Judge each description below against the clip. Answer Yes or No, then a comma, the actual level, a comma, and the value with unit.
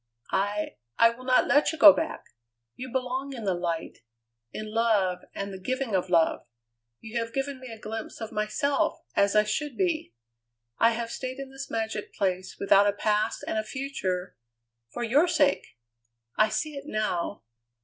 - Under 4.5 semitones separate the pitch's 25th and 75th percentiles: No, average, 4.8 semitones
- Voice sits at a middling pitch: No, high, 225 Hz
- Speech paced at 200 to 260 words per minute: No, average, 175 wpm